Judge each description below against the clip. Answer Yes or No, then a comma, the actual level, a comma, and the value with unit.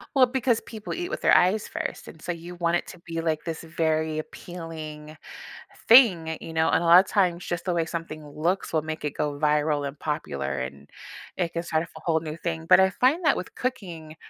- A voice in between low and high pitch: Yes, medium, 165 Hz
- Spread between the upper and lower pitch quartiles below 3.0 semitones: Yes, narrow, 2.6 semitones